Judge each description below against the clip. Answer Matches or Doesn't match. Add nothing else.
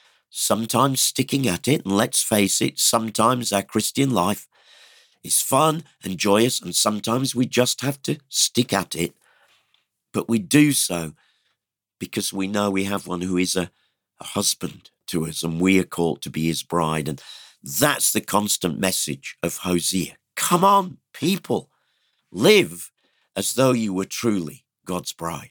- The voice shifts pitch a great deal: Matches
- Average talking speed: Matches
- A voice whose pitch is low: Matches